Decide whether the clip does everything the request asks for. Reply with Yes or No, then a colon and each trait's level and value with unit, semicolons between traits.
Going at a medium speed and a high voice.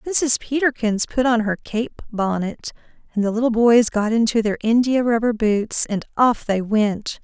Yes: average, 175 wpm; high, 225 Hz